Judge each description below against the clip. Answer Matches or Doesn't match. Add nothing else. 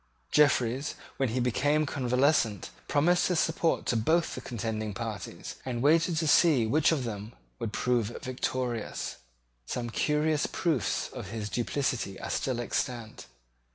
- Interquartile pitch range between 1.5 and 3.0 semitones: Doesn't match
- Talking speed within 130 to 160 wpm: Matches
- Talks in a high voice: Doesn't match